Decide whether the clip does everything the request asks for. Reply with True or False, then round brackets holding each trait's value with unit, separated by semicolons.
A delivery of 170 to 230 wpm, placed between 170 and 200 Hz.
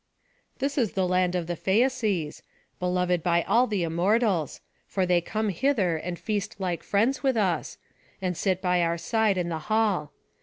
True (175 wpm; 185 Hz)